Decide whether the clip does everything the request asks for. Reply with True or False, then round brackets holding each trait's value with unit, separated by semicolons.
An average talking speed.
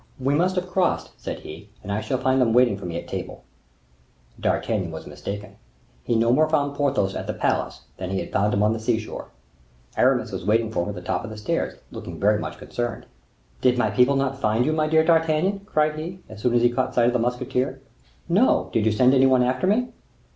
False (235 wpm)